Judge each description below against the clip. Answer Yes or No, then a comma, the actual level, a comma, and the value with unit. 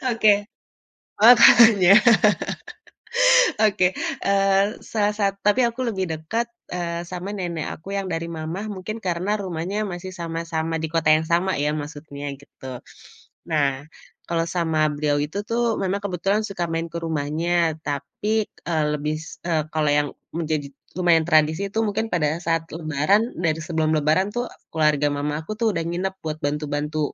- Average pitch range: Yes, average, 4.2 semitones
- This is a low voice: No, medium, 170 Hz